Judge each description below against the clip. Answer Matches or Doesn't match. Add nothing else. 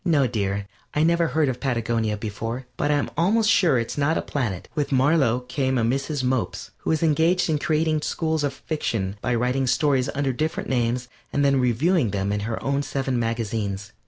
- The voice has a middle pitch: Doesn't match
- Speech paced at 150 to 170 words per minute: Doesn't match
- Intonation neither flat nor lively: Matches